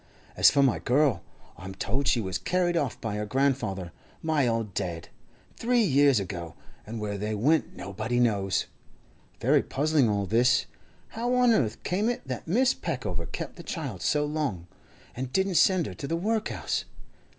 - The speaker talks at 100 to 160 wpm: No, average, 170 wpm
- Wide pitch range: Yes, wide, 7.7 semitones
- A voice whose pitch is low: Yes, low, 130 Hz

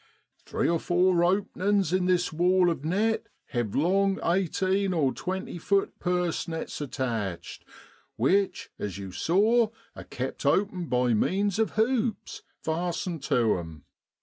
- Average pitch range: Yes, average, 5.0 semitones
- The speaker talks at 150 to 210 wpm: No, average, 140 wpm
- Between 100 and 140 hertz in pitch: No, medium, 180 Hz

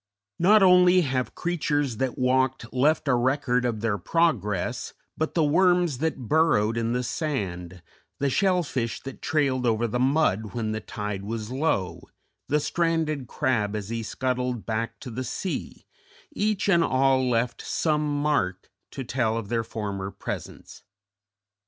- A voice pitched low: Yes, low, 130 Hz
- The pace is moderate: Yes, average, 150 wpm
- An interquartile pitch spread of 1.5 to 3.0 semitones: No, average, 5.3 semitones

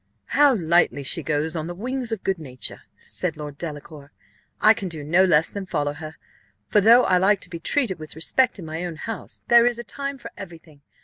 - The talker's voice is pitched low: No, medium, 175 Hz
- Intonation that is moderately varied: No, wide, 6.2 semitones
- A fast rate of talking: Yes, fast, 225 wpm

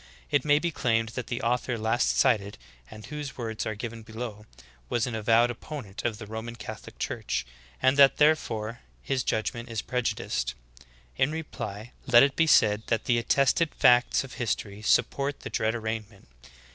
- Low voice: Yes, low, 115 Hz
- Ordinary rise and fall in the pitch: Yes, average, 3.0 semitones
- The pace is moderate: Yes, average, 170 wpm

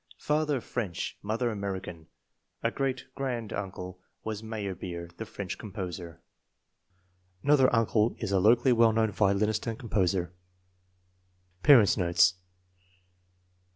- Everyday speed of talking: No, slow, 115 wpm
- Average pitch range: Yes, average, 3.9 semitones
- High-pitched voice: No, low, 105 Hz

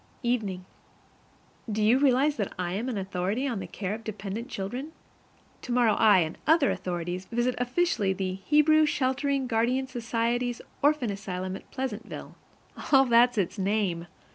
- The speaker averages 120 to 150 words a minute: Yes, average, 145 wpm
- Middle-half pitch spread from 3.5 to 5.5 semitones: Yes, average, 5.1 semitones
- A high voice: Yes, high, 230 Hz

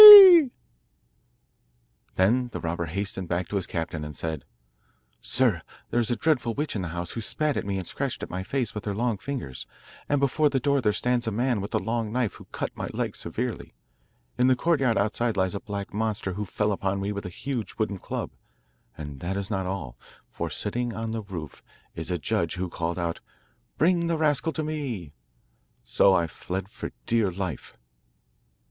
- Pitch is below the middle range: Yes, low, 105 Hz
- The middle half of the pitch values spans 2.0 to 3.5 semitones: No, average, 5.2 semitones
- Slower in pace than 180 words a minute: No, average, 190 wpm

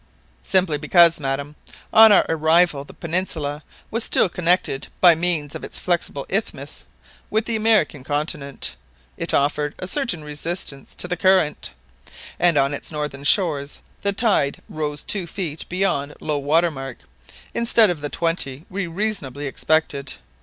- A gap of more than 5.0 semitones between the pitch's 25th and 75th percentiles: No, average, 4.0 semitones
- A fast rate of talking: No, average, 145 wpm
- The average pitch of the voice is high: No, medium, 160 Hz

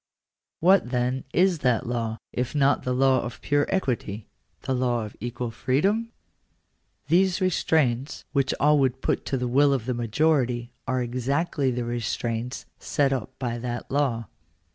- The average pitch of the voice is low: Yes, low, 130 Hz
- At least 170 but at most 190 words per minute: No, average, 160 wpm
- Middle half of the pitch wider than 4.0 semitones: No, average, 3.2 semitones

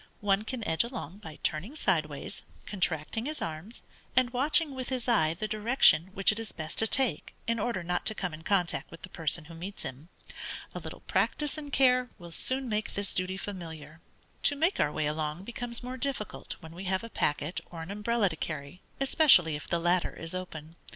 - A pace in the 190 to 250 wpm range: Yes, fast, 205 wpm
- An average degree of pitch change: No, wide, 6.6 semitones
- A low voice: No, high, 190 Hz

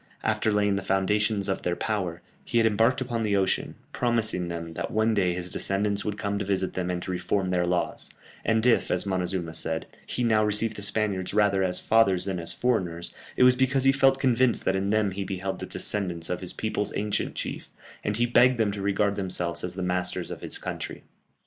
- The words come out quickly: Yes, fast, 215 wpm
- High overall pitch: No, low, 100 Hz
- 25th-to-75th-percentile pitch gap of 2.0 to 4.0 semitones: Yes, average, 3.3 semitones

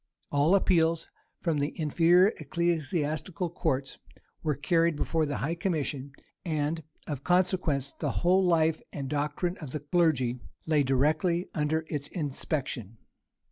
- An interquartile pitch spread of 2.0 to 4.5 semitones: Yes, average, 3.0 semitones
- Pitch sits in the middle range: Yes, medium, 155 Hz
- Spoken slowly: Yes, slow, 130 wpm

